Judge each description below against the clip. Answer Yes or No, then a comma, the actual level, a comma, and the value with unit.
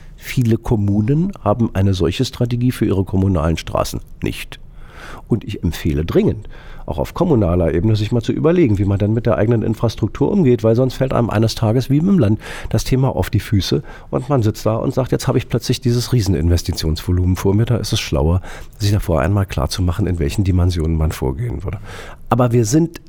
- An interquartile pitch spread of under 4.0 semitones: No, average, 4.8 semitones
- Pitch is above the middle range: No, low, 110 Hz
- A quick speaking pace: Yes, fast, 195 wpm